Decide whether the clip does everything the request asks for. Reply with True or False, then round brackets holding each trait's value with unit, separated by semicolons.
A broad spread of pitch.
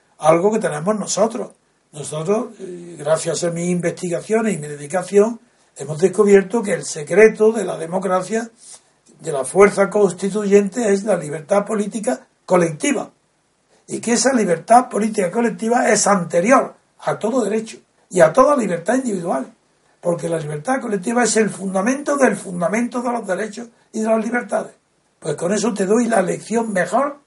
False (4.3 semitones)